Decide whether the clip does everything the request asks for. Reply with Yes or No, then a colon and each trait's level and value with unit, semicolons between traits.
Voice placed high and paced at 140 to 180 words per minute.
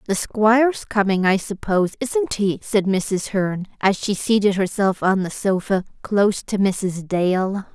Yes: high, 200 Hz; average, 165 wpm